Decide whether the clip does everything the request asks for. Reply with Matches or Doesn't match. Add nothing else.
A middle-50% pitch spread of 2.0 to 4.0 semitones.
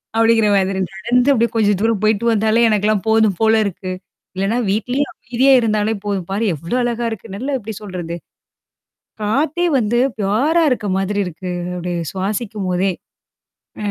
Matches